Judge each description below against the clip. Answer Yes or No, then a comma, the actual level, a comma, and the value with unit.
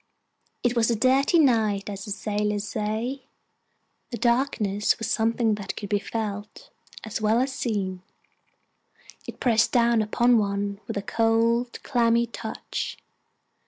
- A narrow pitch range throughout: Yes, narrow, 2.3 semitones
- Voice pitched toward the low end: No, high, 225 Hz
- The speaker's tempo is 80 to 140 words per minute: Yes, slow, 135 wpm